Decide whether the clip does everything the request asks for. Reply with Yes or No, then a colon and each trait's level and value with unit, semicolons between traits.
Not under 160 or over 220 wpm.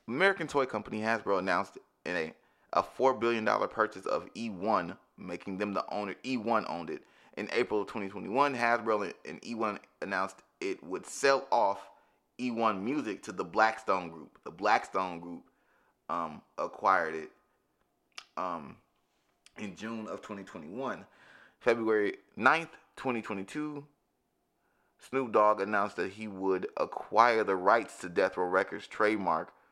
No: slow, 135 wpm